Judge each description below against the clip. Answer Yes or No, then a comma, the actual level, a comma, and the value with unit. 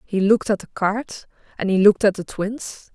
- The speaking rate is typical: No, fast, 225 wpm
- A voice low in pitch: No, high, 205 Hz